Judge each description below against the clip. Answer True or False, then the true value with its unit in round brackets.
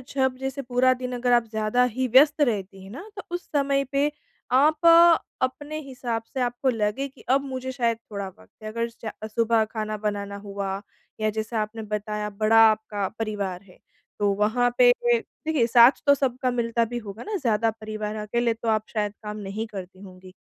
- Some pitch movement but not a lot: True (3.5 semitones)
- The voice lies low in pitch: False (230 Hz)